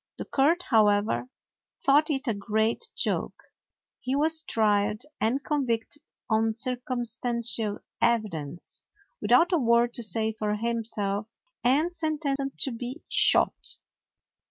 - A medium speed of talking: No, slow, 115 wpm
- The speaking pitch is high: Yes, high, 235 Hz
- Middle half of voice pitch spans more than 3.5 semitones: Yes, average, 4.1 semitones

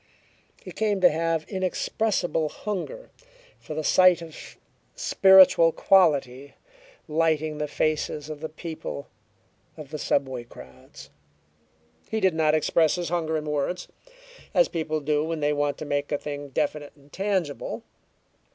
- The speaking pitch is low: No, medium, 155 Hz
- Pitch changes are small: No, average, 3.2 semitones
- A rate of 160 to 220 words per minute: No, average, 140 wpm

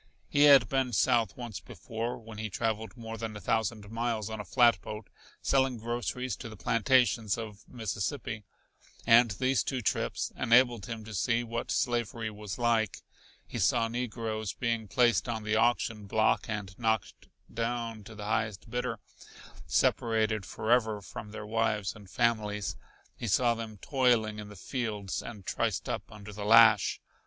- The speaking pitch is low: Yes, low, 110 Hz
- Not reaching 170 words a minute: Yes, average, 160 wpm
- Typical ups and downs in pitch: No, narrow, 1.9 semitones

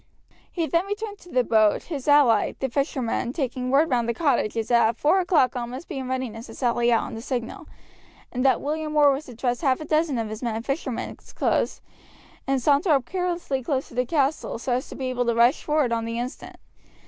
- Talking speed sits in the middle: No, fast, 230 wpm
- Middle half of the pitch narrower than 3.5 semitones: No, average, 4.1 semitones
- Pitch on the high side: Yes, very high, 260 Hz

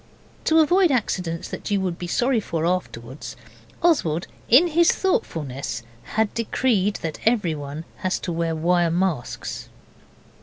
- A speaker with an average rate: No, slow, 130 wpm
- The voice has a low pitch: No, medium, 180 Hz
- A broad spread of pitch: Yes, wide, 6.7 semitones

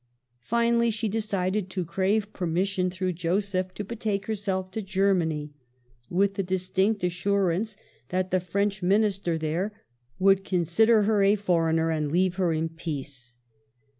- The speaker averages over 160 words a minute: No, slow, 135 wpm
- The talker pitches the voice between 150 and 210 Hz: Yes, high, 190 Hz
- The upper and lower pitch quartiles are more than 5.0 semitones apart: No, average, 2.7 semitones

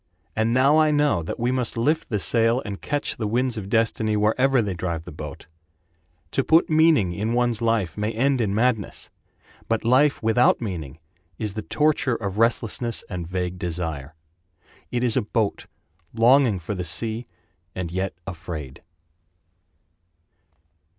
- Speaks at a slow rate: No, average, 155 wpm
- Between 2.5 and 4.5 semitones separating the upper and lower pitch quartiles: No, average, 5.1 semitones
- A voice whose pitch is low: Yes, low, 110 Hz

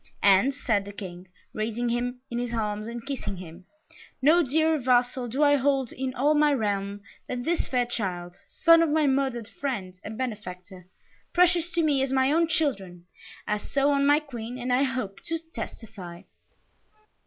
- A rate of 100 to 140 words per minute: No, average, 175 wpm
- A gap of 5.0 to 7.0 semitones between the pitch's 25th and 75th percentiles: Yes, wide, 5.5 semitones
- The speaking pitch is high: Yes, high, 245 Hz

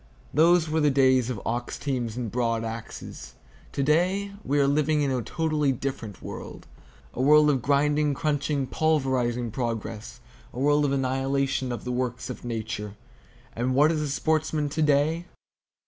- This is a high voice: No, low, 135 Hz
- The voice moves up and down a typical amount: Yes, average, 3.7 semitones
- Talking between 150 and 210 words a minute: Yes, average, 160 wpm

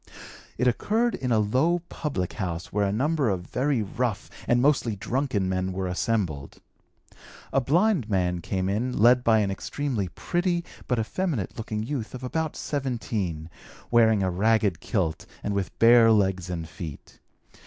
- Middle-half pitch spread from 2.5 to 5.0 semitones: No, wide, 5.4 semitones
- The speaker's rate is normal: Yes, average, 155 wpm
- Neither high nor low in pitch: No, low, 110 Hz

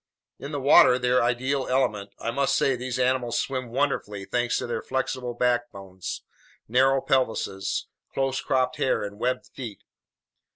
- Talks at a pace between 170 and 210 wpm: No, average, 150 wpm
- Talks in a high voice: No, low, 125 Hz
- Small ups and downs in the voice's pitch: Yes, narrow, 2.1 semitones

